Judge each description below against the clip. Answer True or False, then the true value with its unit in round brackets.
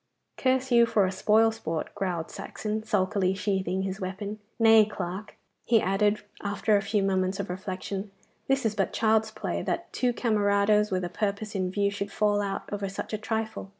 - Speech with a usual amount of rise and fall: False (2.2 semitones)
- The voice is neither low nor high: False (205 Hz)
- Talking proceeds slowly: False (185 wpm)